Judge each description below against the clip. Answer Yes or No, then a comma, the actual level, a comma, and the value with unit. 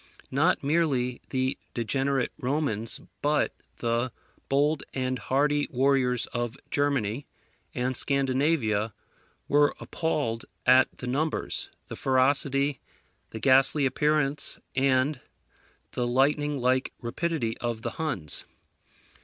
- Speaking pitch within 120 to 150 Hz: Yes, low, 135 Hz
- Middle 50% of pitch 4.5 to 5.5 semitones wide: No, average, 2.8 semitones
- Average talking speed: No, slow, 105 wpm